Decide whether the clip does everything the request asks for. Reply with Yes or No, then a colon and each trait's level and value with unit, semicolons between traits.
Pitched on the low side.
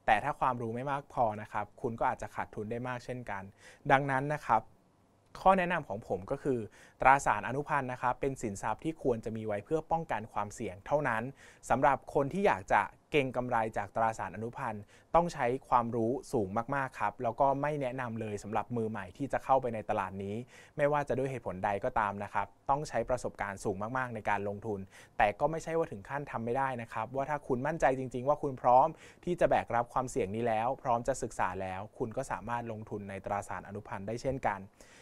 Yes: low, 120 Hz